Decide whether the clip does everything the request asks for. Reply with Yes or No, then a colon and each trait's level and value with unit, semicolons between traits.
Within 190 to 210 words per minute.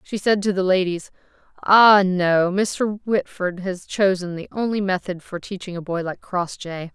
No: average, 175 wpm